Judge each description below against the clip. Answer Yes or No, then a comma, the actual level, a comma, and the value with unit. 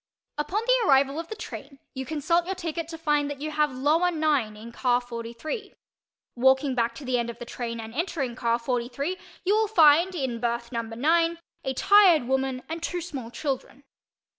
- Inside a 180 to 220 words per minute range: Yes, average, 190 wpm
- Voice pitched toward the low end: No, very high, 280 Hz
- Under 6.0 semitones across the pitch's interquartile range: Yes, wide, 5.4 semitones